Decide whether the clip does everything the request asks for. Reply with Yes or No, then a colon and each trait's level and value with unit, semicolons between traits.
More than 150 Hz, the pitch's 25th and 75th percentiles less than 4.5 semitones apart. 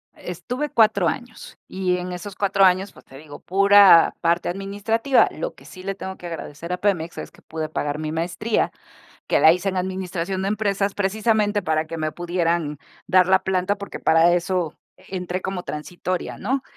Yes: medium, 185 Hz; average, 2.8 semitones